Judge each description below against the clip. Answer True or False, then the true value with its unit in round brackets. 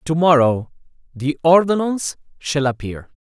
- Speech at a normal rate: False (110 wpm)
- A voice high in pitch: False (150 Hz)